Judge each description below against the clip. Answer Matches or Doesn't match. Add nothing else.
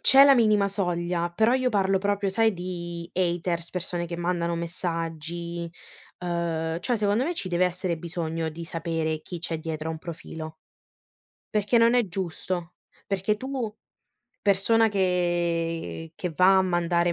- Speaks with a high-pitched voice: Doesn't match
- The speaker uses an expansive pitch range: Doesn't match